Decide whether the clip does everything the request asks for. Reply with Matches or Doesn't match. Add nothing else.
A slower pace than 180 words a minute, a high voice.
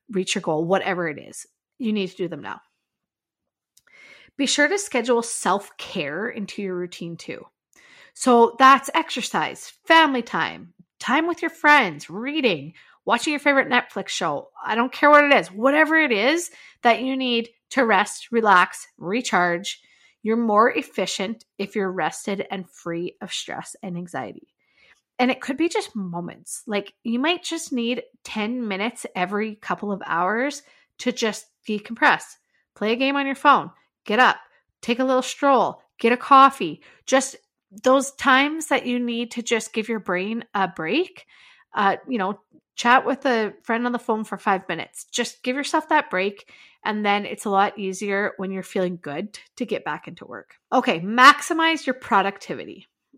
Matches